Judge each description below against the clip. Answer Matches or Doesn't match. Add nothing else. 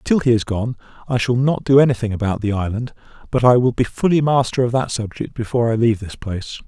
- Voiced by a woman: Doesn't match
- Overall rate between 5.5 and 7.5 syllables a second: Matches